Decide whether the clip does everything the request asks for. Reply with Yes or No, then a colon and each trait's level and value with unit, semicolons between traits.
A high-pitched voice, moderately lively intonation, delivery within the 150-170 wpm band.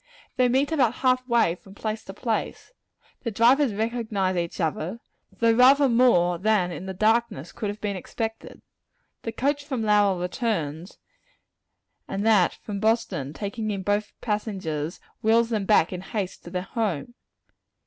Yes: high, 215 Hz; average, 3.9 semitones; average, 160 wpm